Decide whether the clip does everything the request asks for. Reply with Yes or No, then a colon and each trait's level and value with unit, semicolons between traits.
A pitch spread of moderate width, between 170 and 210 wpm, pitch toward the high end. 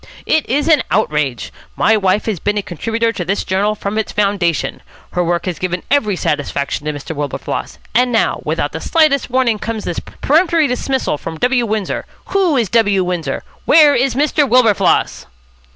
No: wide, 6.3 semitones; average, 175 wpm; high, 215 Hz